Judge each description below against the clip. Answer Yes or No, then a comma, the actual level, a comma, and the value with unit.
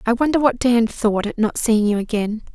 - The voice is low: No, high, 230 Hz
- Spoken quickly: Yes, fast, 235 wpm